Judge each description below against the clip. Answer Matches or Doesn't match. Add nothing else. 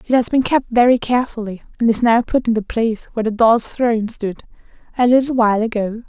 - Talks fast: Matches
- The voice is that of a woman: Matches